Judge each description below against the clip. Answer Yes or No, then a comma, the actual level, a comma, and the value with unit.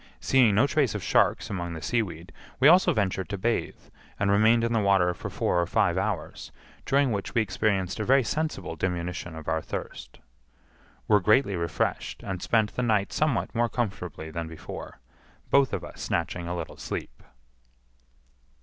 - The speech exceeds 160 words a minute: Yes, average, 170 wpm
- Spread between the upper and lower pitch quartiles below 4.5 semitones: No, average, 5.0 semitones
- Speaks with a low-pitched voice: Yes, low, 100 Hz